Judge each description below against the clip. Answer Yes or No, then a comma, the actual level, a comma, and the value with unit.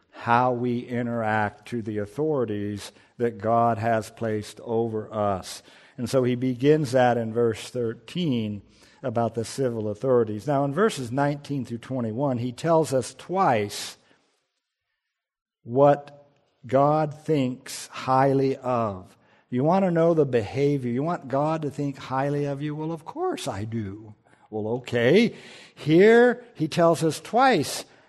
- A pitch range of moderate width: Yes, average, 4.0 semitones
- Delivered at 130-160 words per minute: Yes, average, 140 wpm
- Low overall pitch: Yes, low, 130 Hz